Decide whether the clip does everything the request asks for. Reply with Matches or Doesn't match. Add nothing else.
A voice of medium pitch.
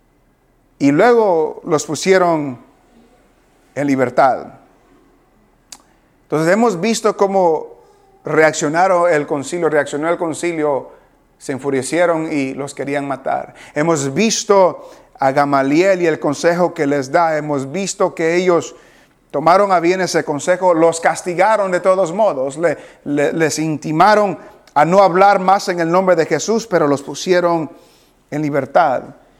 Matches